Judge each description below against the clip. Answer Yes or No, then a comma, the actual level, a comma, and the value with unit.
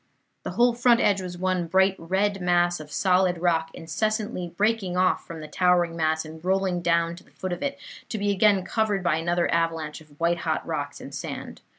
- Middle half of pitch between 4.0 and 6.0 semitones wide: No, average, 2.8 semitones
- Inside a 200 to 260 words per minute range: Yes, fast, 205 wpm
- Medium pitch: Yes, medium, 180 Hz